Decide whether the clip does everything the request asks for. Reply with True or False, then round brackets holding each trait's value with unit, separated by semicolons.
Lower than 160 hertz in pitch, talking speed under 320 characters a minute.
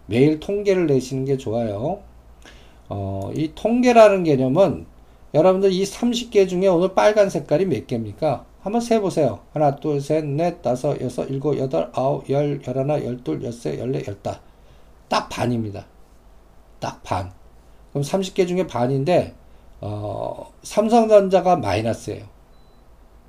True (135 Hz; 265 characters per minute)